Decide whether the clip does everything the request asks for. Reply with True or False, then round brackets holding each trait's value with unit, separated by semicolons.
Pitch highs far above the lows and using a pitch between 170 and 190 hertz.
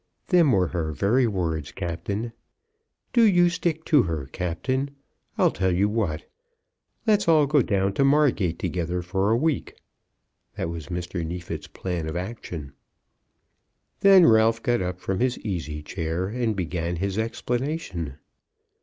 False (6.8 semitones; 95 Hz)